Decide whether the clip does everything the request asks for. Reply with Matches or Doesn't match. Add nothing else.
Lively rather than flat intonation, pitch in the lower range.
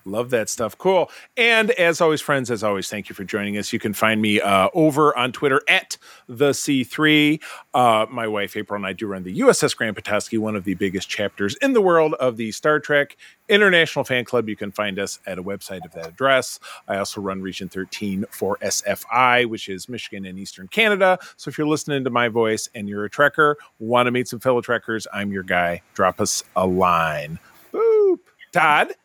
Matches